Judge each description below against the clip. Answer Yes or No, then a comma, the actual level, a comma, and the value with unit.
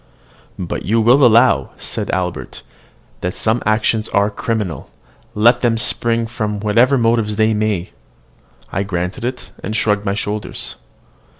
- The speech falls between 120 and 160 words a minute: Yes, slow, 135 wpm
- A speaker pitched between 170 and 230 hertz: No, low, 110 Hz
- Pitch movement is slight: Yes, narrow, 2.1 semitones